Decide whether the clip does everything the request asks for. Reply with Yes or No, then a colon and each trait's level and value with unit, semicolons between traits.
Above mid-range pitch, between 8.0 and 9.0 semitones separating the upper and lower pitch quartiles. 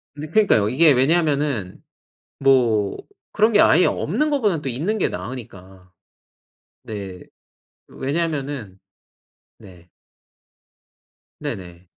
No: low, 135 Hz; wide, 8.6 semitones